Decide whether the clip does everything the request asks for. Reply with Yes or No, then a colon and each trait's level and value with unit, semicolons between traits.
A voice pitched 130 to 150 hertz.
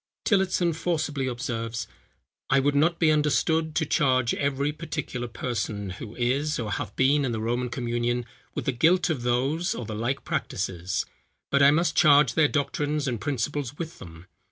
Yes: low, 135 Hz